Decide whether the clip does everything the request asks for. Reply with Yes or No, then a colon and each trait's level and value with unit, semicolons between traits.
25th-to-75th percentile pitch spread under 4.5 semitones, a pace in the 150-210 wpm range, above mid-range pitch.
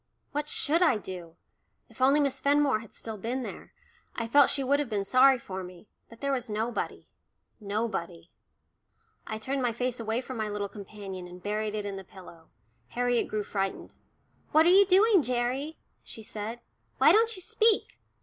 No: average, 5.1 semitones; average, 180 wpm; high, 230 Hz